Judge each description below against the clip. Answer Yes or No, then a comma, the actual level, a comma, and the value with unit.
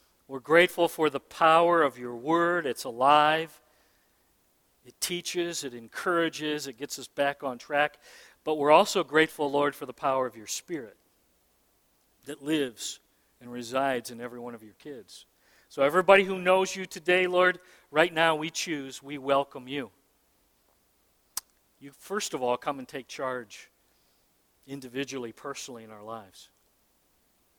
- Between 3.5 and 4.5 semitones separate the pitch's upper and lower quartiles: Yes, average, 4.0 semitones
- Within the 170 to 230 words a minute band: No, average, 150 wpm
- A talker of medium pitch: Yes, medium, 145 Hz